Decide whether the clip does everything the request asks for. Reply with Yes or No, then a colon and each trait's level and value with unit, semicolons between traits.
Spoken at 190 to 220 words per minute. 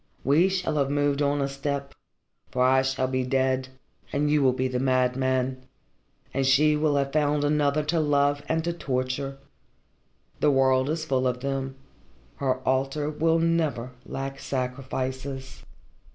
No: average, 150 wpm